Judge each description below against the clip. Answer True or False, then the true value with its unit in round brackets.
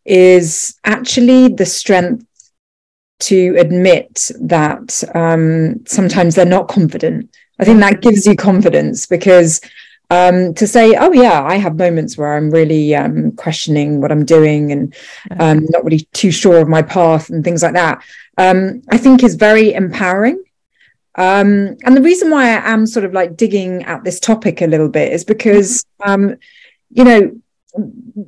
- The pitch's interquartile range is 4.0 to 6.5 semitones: True (4.7 semitones)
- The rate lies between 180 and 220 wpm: False (160 wpm)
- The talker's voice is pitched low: False (185 Hz)